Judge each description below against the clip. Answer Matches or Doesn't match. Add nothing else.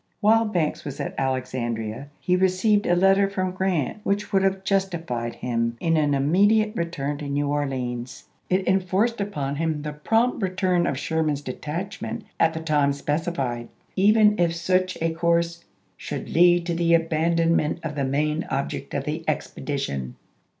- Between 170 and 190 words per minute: Doesn't match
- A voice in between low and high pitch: Matches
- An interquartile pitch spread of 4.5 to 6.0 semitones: Matches